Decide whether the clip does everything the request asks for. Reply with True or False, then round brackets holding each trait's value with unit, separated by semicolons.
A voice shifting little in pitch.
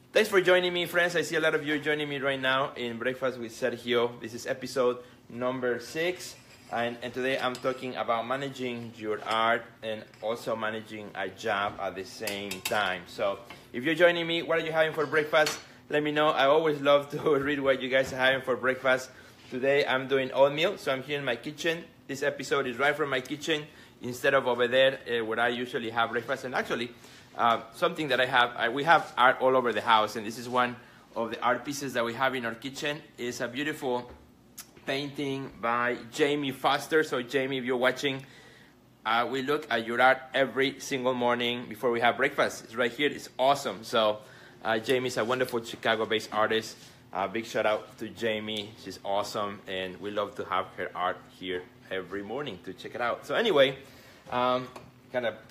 False (3.0 semitones)